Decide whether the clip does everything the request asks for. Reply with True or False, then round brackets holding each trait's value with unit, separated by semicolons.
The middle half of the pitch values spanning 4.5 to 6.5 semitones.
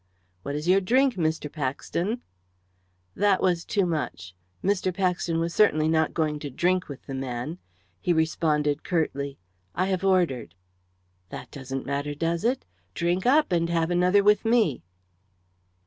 False (4.1 semitones)